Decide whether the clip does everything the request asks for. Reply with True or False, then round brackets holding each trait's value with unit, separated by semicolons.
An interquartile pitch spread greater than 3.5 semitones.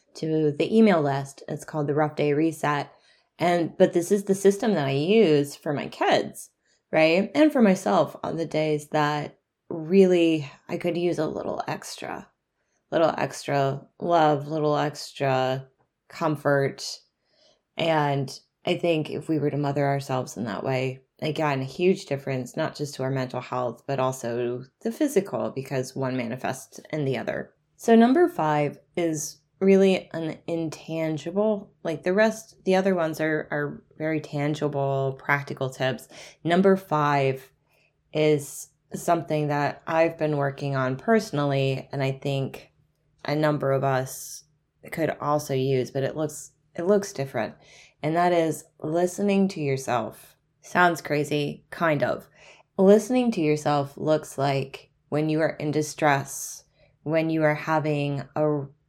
False (3.2 semitones)